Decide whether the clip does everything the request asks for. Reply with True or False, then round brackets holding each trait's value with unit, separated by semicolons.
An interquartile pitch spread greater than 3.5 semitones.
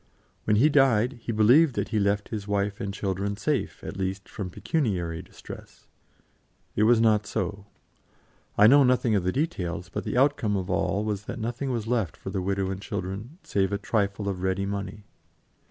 False (3.2 semitones)